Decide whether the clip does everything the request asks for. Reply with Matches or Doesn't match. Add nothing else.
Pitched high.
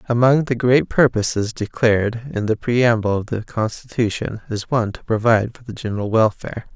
Doesn't match